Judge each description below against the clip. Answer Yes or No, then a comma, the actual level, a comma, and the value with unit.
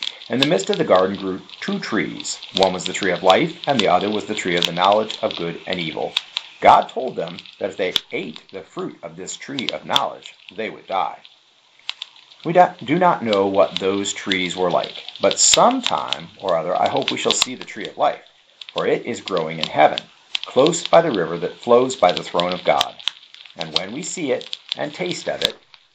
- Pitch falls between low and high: No, very low, 95 Hz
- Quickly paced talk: Yes, fast, 215 wpm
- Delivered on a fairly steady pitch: No, average, 3.7 semitones